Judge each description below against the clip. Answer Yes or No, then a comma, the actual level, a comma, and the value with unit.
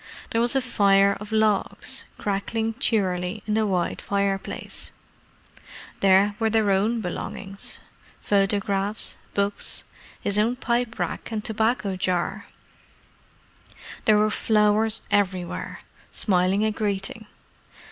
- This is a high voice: Yes, high, 205 Hz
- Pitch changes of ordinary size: No, narrow, 2.0 semitones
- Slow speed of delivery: Yes, slow, 105 wpm